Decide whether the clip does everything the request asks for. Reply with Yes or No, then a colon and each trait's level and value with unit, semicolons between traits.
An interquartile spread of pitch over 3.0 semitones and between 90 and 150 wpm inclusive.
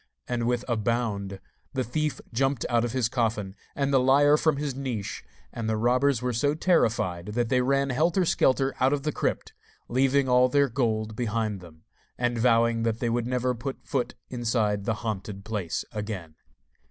No: average, 3.4 semitones; average, 180 wpm